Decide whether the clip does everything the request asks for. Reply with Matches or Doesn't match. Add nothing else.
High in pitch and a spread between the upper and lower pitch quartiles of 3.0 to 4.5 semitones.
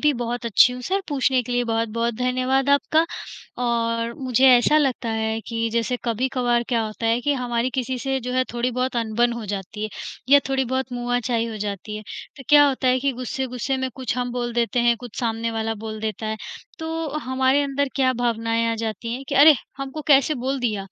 Doesn't match